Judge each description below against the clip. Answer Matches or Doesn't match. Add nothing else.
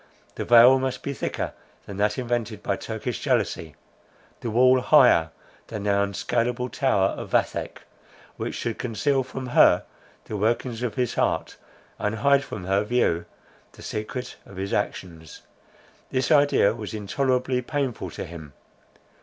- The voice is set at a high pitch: Doesn't match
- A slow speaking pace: Doesn't match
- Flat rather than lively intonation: Doesn't match